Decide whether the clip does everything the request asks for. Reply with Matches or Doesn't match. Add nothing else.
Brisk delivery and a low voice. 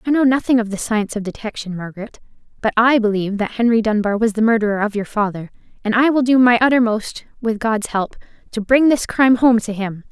Doesn't match